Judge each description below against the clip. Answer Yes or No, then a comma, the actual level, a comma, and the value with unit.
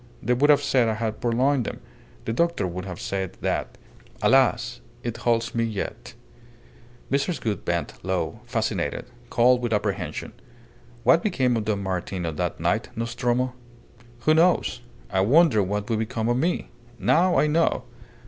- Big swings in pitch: No, average, 4.5 semitones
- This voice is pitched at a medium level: No, low, 115 Hz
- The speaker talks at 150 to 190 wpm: Yes, average, 160 wpm